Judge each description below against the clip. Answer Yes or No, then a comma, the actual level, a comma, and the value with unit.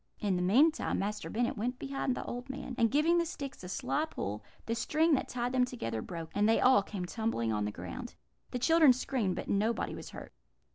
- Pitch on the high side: Yes, high, 240 Hz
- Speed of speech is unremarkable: No, fast, 220 wpm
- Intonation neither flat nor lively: No, wide, 6.0 semitones